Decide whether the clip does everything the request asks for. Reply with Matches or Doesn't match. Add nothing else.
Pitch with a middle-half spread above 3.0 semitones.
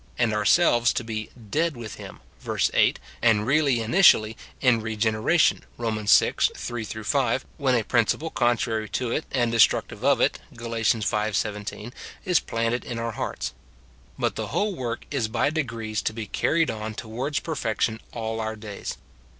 Doesn't match